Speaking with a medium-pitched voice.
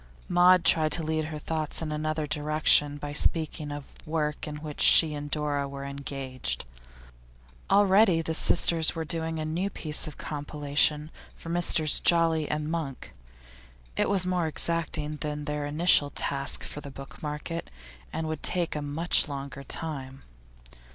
Yes: medium, 155 Hz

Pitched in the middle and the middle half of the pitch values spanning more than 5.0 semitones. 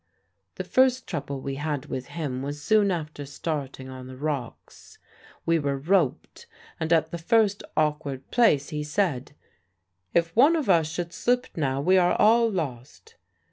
Yes: medium, 155 Hz; wide, 5.4 semitones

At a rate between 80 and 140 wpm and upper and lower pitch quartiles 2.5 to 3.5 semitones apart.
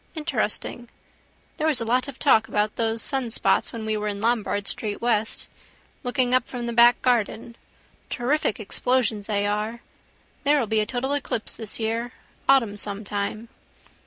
No: average, 160 wpm; average, 2.8 semitones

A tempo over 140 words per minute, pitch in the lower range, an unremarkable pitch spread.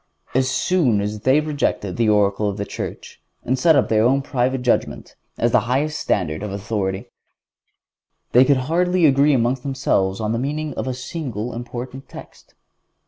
Yes: average, 170 wpm; low, 125 Hz; average, 4.5 semitones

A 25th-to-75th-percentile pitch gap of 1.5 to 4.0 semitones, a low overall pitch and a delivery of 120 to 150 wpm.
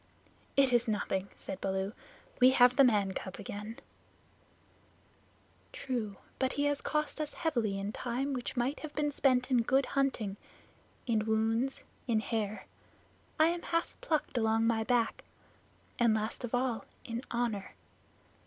No: average, 3.7 semitones; high, 240 Hz; average, 145 wpm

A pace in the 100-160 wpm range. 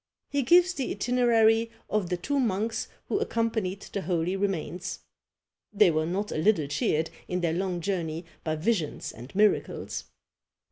Yes: average, 150 wpm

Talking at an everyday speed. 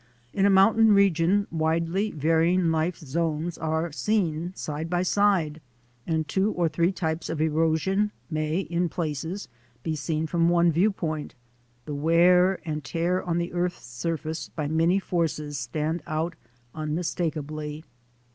Yes: average, 145 wpm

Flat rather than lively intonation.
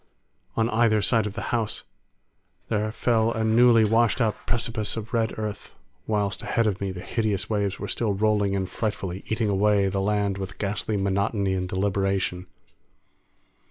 Yes: narrow, 2.2 semitones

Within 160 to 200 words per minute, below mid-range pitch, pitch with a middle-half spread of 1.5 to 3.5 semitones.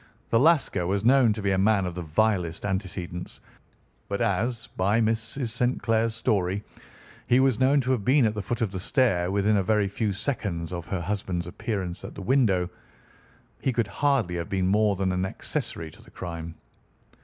No: average, 190 wpm; low, 100 Hz; average, 4.0 semitones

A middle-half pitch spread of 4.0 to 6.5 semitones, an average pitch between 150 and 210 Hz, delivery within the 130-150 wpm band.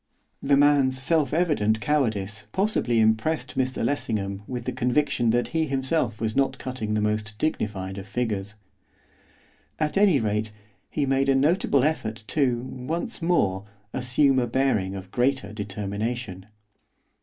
No: average, 4.7 semitones; low, 125 Hz; average, 140 wpm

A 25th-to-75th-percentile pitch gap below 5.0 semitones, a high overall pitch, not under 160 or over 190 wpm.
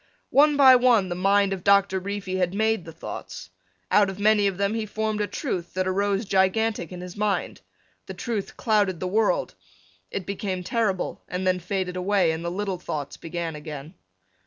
Yes: narrow, 2.5 semitones; high, 195 Hz; average, 185 wpm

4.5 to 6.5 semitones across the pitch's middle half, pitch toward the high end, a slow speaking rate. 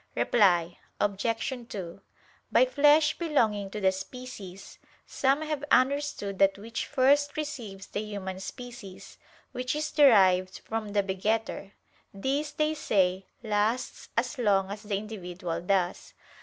Yes: wide, 5.5 semitones; high, 215 Hz; slow, 130 wpm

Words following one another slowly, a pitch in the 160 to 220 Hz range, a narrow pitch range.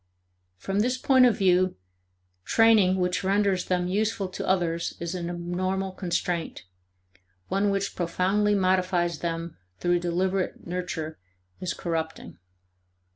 Yes: slow, 120 wpm; medium, 185 Hz; narrow, 2.1 semitones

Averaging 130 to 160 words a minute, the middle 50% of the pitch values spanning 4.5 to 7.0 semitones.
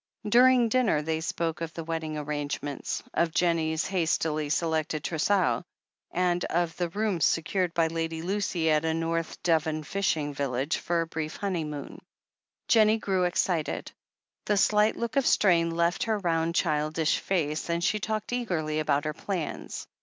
No: average, 155 wpm; average, 3.3 semitones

